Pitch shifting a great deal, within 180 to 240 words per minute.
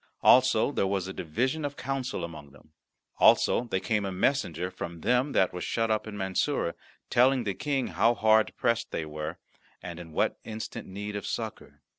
Yes: wide, 5.7 semitones; average, 185 wpm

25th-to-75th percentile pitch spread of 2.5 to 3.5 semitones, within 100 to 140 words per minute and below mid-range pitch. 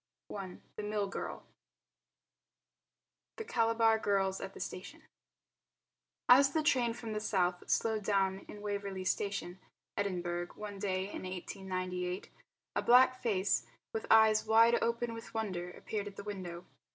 No: average, 3.1 semitones; slow, 135 wpm; high, 205 Hz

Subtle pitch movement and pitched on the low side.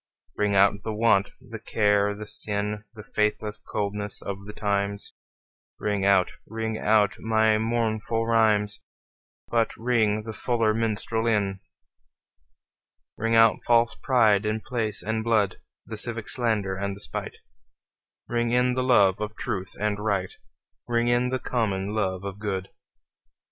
Yes: narrow, 2.0 semitones; low, 110 Hz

